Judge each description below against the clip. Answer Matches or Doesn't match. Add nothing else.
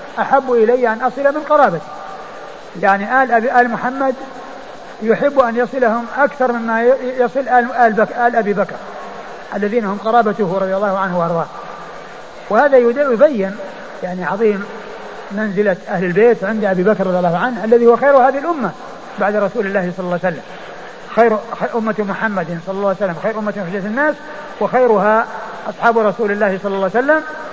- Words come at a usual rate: Doesn't match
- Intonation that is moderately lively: Matches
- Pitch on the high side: Matches